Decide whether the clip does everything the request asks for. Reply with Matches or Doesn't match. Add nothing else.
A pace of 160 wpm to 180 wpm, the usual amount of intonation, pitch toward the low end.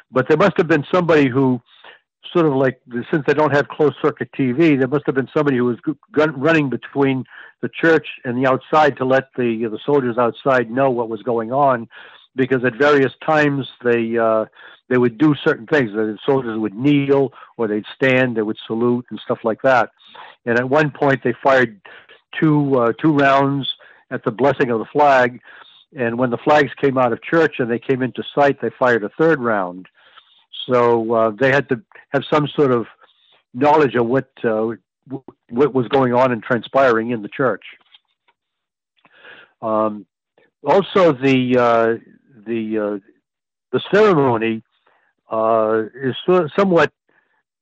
Matches